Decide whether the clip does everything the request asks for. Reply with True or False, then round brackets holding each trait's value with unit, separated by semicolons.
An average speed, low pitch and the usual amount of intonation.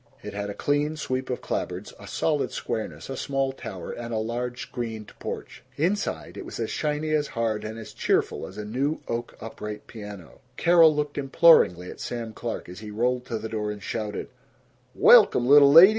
True (190 wpm; 120 Hz; 5.0 semitones)